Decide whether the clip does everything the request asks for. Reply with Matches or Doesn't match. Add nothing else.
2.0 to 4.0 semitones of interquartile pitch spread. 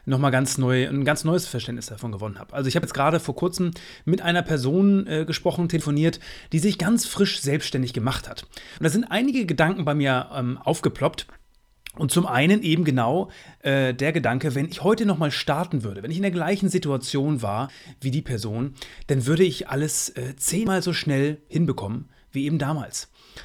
Doesn't match